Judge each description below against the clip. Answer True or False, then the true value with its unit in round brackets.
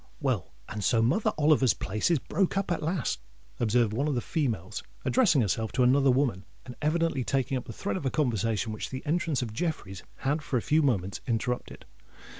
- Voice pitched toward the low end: True (130 Hz)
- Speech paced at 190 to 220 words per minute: True (200 wpm)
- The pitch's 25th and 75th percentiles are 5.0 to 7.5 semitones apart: True (5.3 semitones)